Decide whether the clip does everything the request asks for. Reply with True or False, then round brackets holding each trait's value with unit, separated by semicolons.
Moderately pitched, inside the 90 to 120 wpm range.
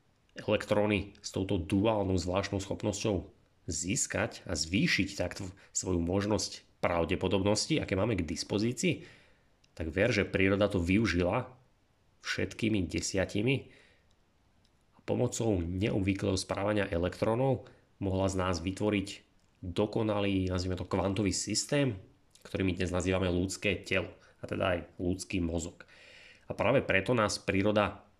False (100 Hz; 115 wpm)